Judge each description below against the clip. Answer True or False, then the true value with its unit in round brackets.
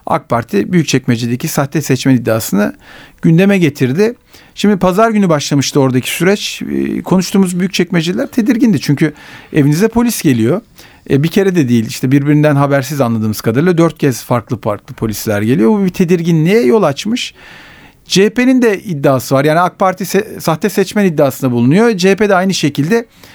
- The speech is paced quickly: True (150 wpm)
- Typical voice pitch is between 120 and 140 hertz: False (165 Hz)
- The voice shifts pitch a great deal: True (6.5 semitones)